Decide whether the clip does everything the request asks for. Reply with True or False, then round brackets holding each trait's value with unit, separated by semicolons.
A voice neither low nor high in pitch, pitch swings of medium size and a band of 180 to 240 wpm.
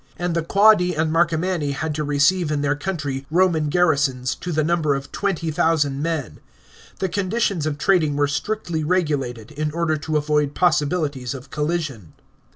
False (155 Hz; 3.2 semitones; 160 wpm)